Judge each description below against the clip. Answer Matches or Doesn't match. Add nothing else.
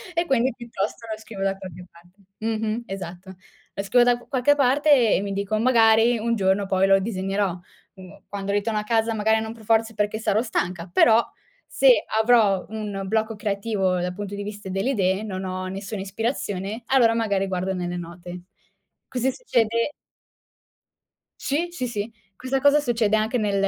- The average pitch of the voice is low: Doesn't match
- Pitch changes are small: Doesn't match